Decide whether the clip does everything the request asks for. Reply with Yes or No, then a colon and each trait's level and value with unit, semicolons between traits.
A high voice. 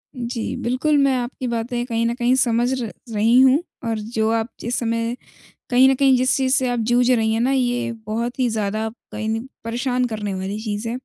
Yes: high, 240 Hz